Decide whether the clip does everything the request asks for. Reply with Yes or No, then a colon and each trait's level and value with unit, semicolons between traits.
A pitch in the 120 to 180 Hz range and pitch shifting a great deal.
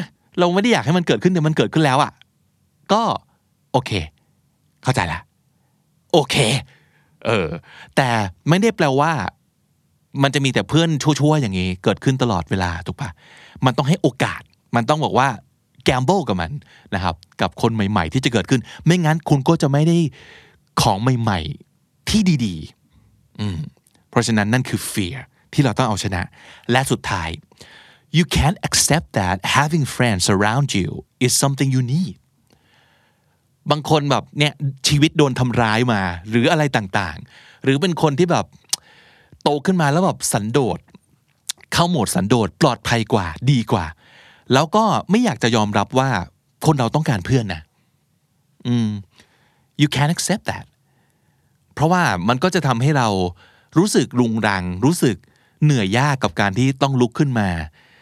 Yes: low, 130 Hz; wide, 5.9 semitones